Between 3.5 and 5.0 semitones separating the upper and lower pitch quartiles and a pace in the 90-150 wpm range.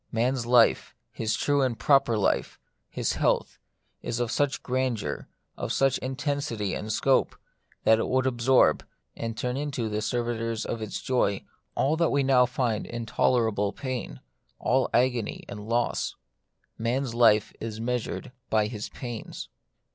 No: average, 2.8 semitones; average, 145 wpm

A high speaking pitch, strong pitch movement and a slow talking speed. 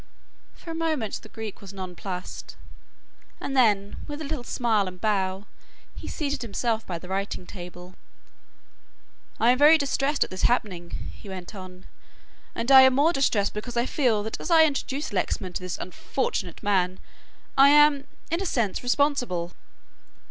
No: high, 220 Hz; wide, 6.7 semitones; average, 165 wpm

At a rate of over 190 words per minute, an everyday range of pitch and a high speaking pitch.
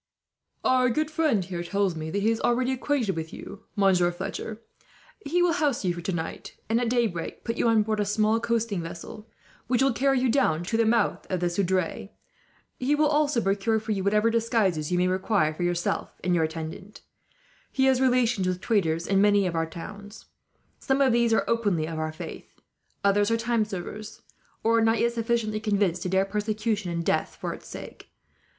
Yes: average, 200 wpm; average, 4.4 semitones; high, 210 Hz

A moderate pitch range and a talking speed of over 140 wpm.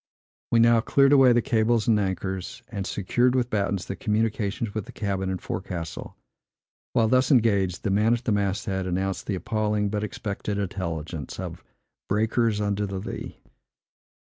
Yes: average, 3.0 semitones; average, 165 wpm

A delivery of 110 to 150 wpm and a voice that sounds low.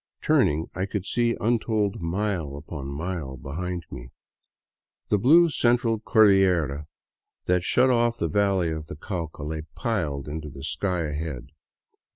Yes: average, 140 wpm; very low, 90 Hz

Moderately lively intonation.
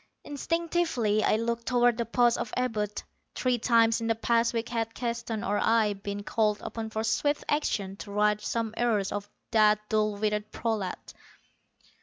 No: narrow, 2.1 semitones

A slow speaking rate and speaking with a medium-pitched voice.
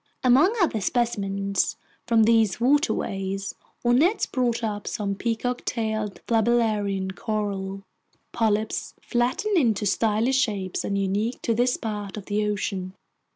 No: slow, 125 wpm; high, 220 Hz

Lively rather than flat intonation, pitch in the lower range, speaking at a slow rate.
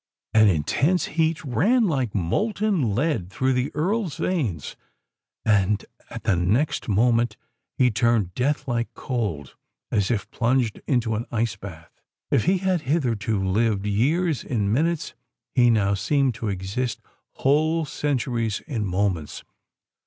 Yes: wide, 6.3 semitones; low, 120 Hz; slow, 130 wpm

